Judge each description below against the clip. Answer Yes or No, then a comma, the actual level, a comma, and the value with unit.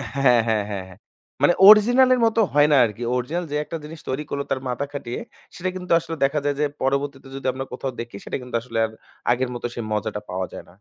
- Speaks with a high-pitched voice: No, low, 135 Hz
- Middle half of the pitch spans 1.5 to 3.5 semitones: No, average, 4.3 semitones